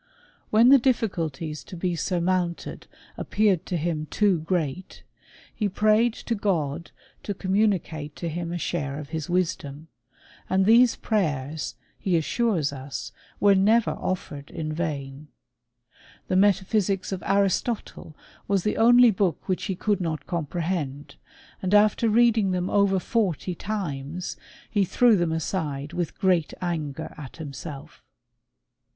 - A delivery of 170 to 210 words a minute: No, slow, 135 wpm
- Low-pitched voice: No, medium, 180 Hz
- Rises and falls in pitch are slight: No, average, 4.6 semitones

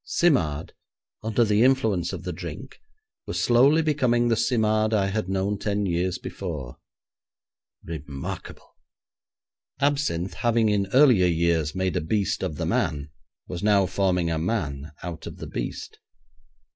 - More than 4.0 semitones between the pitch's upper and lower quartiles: Yes, average, 5.2 semitones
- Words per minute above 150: No, average, 140 wpm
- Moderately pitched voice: No, very low, 95 Hz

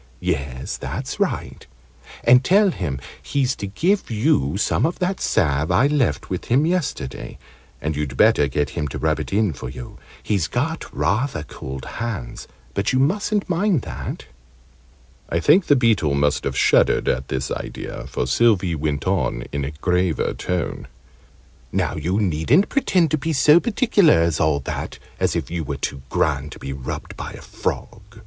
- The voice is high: No, very low, 90 Hz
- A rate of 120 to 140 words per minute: No, average, 170 wpm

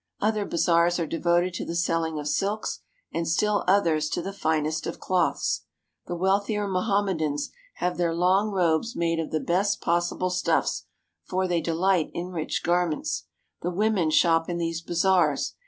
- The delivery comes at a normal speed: Yes, average, 170 wpm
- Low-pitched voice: No, medium, 175 Hz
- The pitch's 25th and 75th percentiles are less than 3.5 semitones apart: Yes, narrow, 2.5 semitones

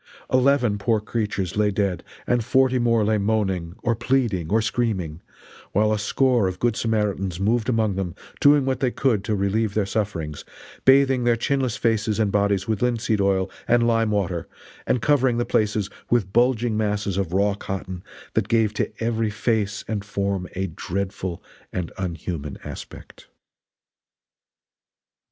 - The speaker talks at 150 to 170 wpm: Yes, average, 155 wpm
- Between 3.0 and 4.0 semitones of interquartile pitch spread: Yes, average, 3.3 semitones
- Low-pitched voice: Yes, low, 105 Hz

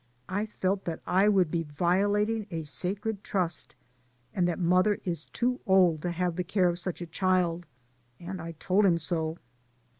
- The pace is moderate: Yes, average, 175 wpm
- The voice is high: No, medium, 180 Hz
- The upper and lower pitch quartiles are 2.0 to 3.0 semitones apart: Yes, narrow, 2.5 semitones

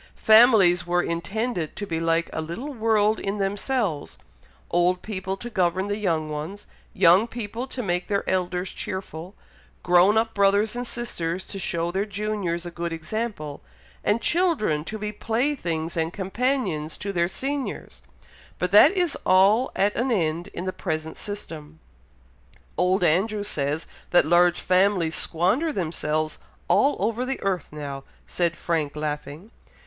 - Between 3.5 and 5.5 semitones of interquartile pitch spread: Yes, average, 4.3 semitones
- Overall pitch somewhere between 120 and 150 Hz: No, high, 190 Hz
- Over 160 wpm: No, average, 150 wpm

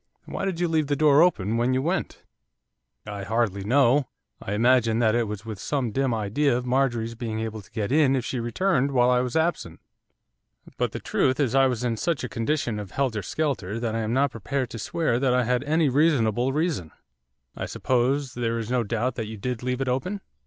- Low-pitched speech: Yes, low, 125 Hz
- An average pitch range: Yes, average, 3.7 semitones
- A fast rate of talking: Yes, fast, 215 wpm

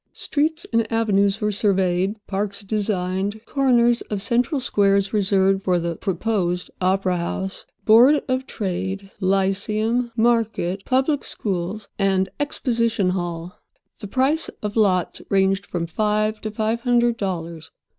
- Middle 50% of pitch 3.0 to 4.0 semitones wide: Yes, average, 3.3 semitones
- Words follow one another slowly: Yes, slow, 125 wpm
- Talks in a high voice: Yes, high, 200 Hz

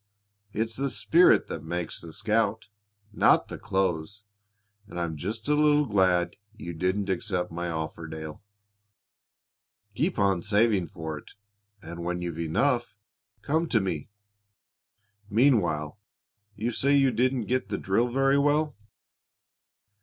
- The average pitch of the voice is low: Yes, low, 100 Hz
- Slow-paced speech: Yes, slow, 130 wpm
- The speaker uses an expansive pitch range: Yes, wide, 6.3 semitones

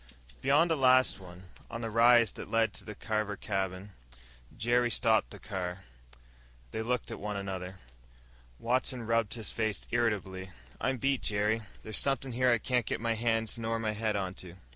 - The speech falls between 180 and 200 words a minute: No, average, 170 wpm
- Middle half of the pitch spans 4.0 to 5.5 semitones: No, average, 2.9 semitones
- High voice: No, low, 115 Hz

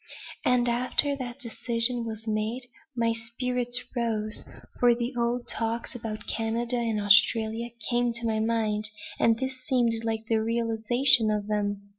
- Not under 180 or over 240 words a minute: No, average, 145 wpm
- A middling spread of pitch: No, narrow, 1.7 semitones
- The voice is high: Yes, high, 230 Hz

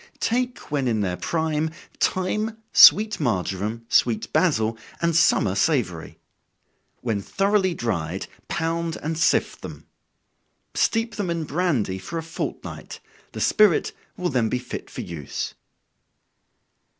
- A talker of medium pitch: Yes, medium, 155 Hz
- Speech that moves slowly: Yes, slow, 125 wpm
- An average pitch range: No, wide, 8.6 semitones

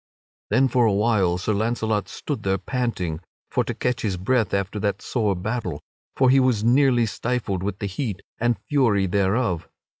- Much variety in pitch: No, average, 4.2 semitones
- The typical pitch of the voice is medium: No, low, 110 Hz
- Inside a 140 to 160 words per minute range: No, average, 175 wpm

